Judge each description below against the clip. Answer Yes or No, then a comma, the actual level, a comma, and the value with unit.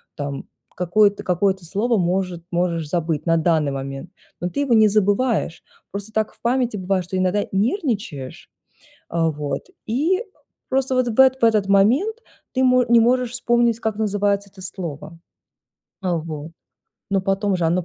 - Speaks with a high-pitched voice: Yes, high, 200 Hz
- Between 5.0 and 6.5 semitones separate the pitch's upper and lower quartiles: Yes, wide, 5.4 semitones